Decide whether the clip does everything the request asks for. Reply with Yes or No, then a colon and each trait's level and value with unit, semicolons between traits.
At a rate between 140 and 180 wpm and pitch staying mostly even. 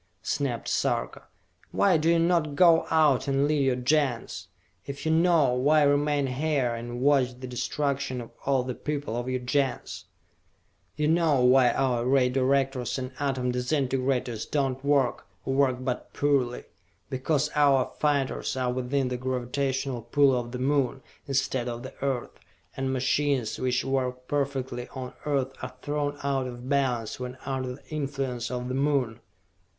Yes: average, 160 wpm; narrow, 2.2 semitones